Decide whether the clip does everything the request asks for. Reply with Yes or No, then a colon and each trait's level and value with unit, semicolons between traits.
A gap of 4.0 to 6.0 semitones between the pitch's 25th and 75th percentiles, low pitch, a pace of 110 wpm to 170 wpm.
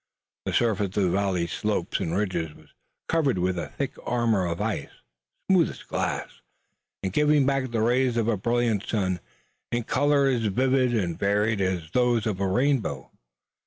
Yes: average, 5.2 semitones; low, 110 Hz; average, 165 wpm